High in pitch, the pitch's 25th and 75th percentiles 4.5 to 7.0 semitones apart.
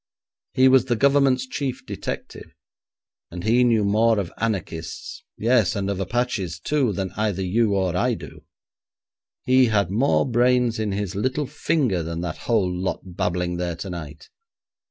No: low, 105 Hz; average, 5.3 semitones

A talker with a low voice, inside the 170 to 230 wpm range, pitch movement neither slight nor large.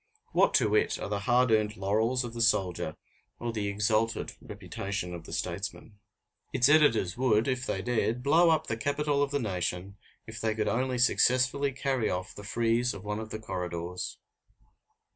Yes: low, 110 Hz; average, 180 wpm; average, 4.0 semitones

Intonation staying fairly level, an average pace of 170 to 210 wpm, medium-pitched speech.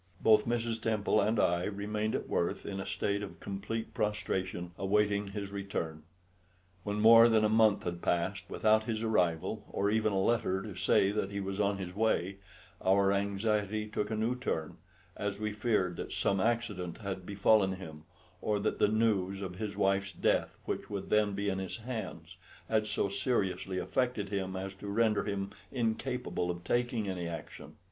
No: narrow, 2.2 semitones; average, 180 wpm; low, 100 Hz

